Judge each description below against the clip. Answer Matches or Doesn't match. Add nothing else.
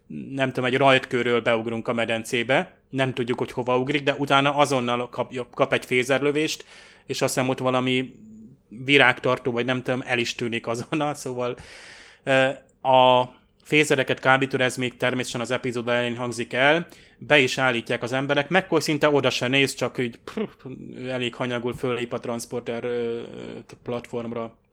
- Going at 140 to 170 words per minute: Matches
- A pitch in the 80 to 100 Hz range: Doesn't match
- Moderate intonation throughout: Doesn't match